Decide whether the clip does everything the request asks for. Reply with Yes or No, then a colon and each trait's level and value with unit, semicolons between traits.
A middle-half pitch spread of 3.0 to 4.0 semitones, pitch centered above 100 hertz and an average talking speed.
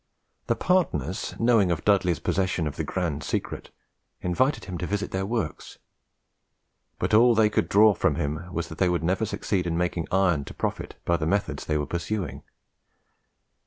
No: average, 3.6 semitones; very low, 90 Hz; average, 175 wpm